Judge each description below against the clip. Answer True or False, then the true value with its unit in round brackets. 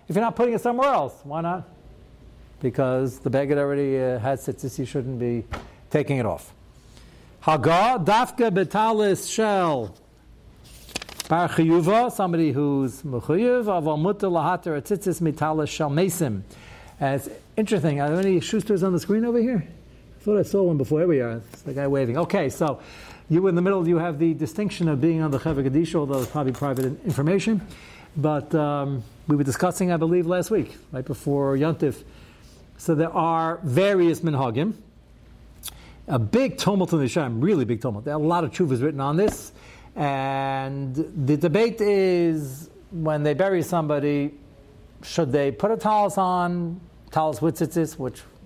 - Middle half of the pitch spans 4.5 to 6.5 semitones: True (4.8 semitones)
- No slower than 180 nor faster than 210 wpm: False (165 wpm)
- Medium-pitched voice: True (160 Hz)